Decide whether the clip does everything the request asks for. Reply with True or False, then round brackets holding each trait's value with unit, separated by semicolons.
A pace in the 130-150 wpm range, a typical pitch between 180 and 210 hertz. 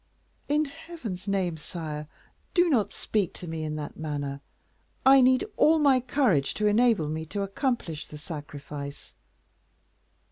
True (140 wpm; 190 Hz)